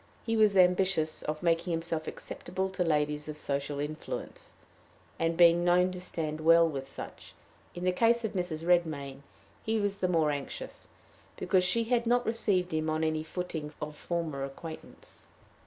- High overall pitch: No, medium, 170 Hz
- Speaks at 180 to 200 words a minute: No, average, 170 wpm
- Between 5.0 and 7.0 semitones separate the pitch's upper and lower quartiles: No, average, 3.0 semitones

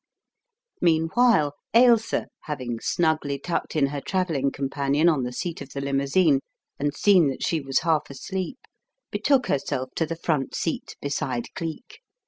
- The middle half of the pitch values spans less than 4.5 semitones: Yes, average, 3.9 semitones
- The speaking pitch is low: No, medium, 150 Hz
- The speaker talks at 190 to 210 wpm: No, average, 145 wpm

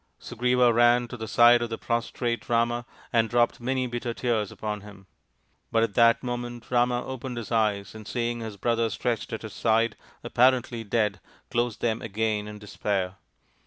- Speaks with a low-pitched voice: Yes, low, 115 Hz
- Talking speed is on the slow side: No, average, 170 wpm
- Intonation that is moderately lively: No, narrow, 1.8 semitones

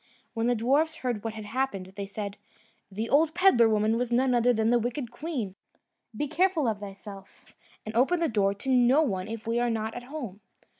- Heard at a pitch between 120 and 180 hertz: No, high, 235 Hz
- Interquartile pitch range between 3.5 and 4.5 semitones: Yes, average, 3.9 semitones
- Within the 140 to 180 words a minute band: No, fast, 205 wpm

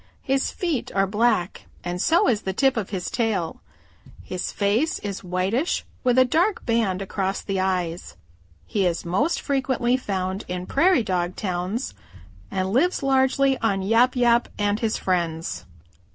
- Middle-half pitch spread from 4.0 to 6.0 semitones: Yes, wide, 5.6 semitones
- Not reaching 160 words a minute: Yes, average, 150 wpm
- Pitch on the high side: Yes, high, 210 Hz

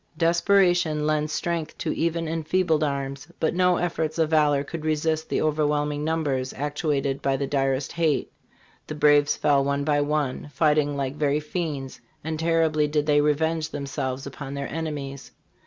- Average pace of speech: Yes, average, 155 wpm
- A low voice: No, medium, 150 Hz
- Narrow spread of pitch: Yes, narrow, 2.2 semitones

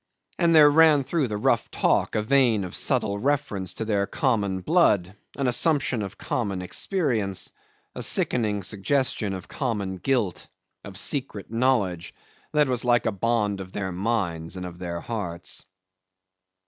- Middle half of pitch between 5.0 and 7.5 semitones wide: Yes, wide, 5.5 semitones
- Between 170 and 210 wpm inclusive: No, average, 150 wpm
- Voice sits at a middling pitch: No, low, 110 Hz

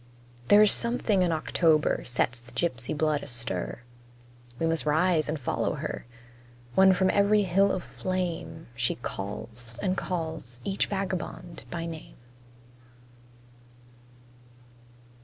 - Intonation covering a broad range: Yes, wide, 7.1 semitones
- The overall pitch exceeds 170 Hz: No, medium, 165 Hz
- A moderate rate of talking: No, slow, 120 wpm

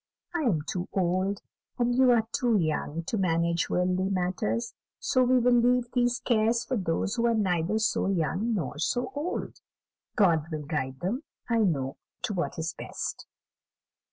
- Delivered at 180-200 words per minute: No, average, 165 wpm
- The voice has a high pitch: Yes, high, 195 Hz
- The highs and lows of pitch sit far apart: Yes, wide, 6.1 semitones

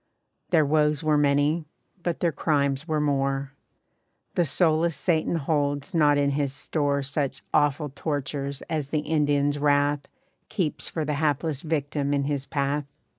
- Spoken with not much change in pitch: Yes, narrow, 1.7 semitones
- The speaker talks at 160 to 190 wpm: No, average, 145 wpm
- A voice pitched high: No, medium, 145 Hz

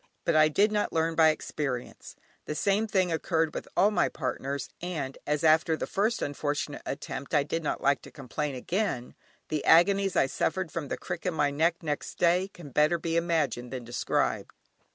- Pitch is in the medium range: Yes, medium, 160 Hz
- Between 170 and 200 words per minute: Yes, average, 190 wpm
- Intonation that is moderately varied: Yes, average, 3.5 semitones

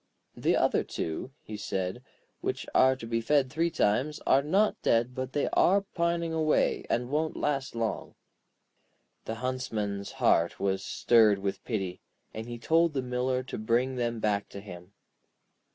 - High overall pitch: No, low, 120 Hz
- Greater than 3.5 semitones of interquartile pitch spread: Yes, average, 4.8 semitones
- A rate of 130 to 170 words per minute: Yes, average, 160 wpm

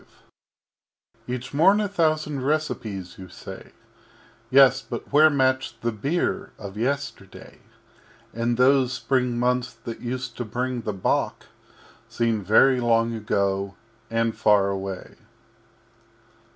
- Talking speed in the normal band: No, slow, 120 wpm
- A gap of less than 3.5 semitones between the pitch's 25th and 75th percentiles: No, average, 3.8 semitones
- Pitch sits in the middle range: No, low, 125 Hz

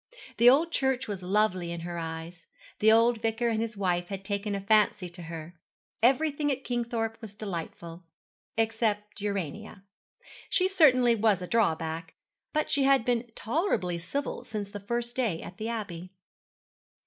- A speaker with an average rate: Yes, average, 160 wpm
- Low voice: No, high, 215 Hz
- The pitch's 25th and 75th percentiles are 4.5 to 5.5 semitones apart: Yes, average, 4.9 semitones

